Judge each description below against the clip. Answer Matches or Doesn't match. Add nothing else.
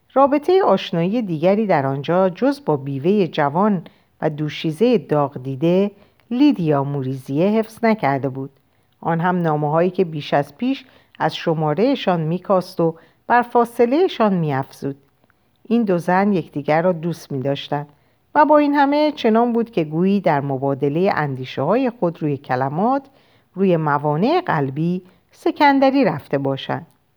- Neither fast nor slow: Matches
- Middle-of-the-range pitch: Matches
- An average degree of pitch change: Doesn't match